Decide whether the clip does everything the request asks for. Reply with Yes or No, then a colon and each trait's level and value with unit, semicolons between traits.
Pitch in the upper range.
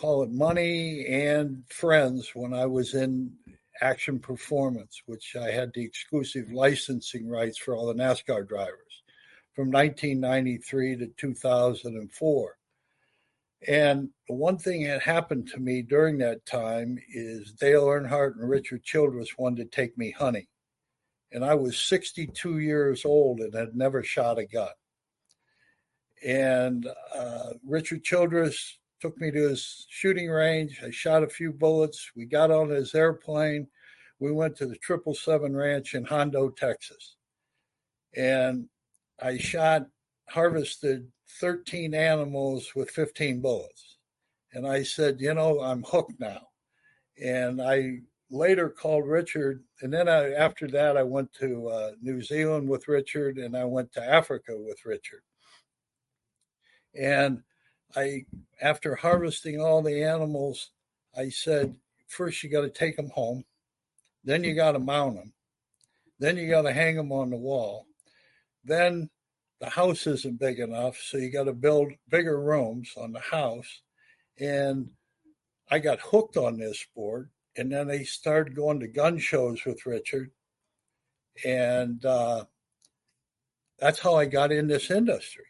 No: medium, 140 Hz